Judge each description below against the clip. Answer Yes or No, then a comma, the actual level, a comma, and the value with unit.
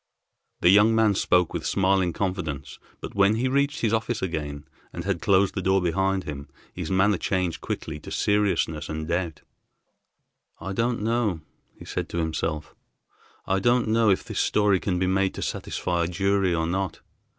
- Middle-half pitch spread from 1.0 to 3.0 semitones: No, average, 3.4 semitones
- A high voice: No, very low, 95 Hz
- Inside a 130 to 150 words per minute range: No, average, 175 wpm